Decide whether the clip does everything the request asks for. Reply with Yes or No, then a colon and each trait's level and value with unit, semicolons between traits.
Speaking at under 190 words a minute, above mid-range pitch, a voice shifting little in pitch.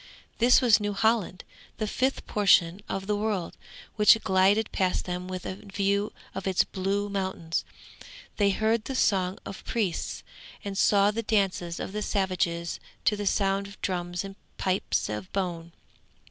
Yes: average, 160 wpm; high, 195 Hz; narrow, 2.1 semitones